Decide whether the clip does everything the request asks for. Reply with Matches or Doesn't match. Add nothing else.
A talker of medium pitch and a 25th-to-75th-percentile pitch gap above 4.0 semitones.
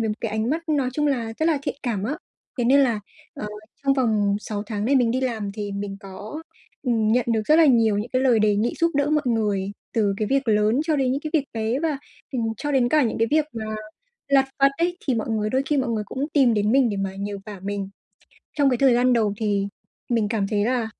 Doesn't match